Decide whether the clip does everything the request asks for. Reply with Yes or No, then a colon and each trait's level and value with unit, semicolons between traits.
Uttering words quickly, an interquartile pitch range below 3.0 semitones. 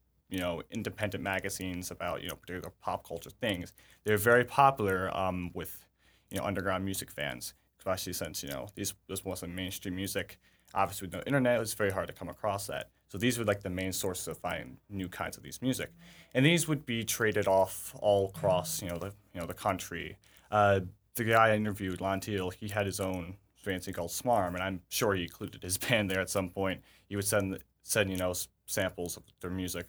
Yes: fast, 215 wpm; narrow, 2.4 semitones